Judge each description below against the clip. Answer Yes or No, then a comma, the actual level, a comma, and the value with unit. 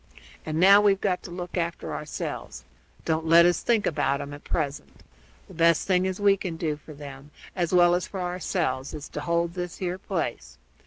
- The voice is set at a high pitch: No, medium, 170 Hz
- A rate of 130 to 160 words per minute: No, average, 200 wpm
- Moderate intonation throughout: Yes, average, 3.2 semitones